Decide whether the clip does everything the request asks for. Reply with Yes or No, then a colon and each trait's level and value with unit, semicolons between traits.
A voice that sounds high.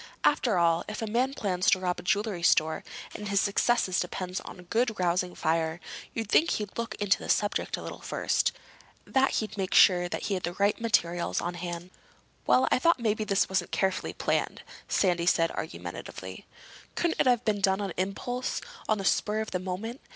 Yes: high, 195 Hz